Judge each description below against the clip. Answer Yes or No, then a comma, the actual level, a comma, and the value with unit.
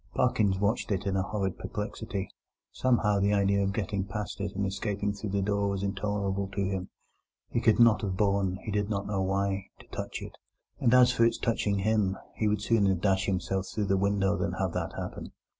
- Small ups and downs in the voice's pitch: Yes, narrow, 1.4 semitones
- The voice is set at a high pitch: No, low, 100 Hz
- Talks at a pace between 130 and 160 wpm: No, average, 195 wpm